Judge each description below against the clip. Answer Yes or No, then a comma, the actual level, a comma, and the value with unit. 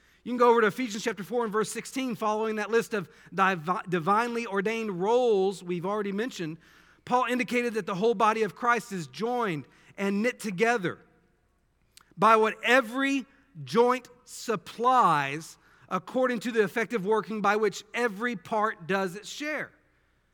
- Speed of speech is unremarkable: Yes, average, 155 wpm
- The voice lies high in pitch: Yes, high, 220 Hz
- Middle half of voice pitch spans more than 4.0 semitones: No, average, 3.4 semitones